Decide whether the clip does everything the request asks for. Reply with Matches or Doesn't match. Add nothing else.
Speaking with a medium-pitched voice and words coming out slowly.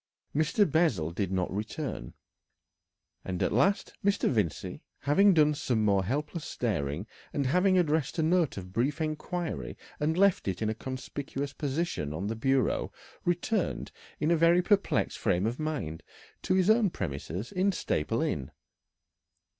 Doesn't match